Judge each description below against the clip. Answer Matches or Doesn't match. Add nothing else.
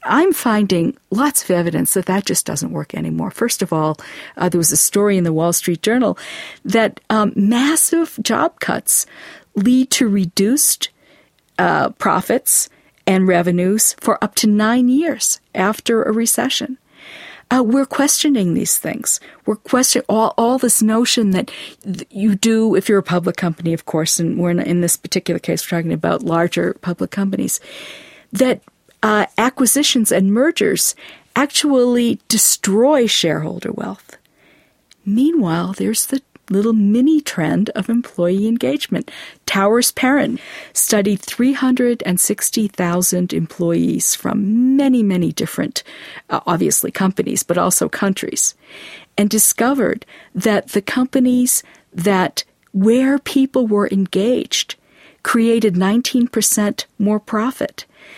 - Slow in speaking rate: Matches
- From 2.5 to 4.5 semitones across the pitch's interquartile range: Doesn't match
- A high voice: Matches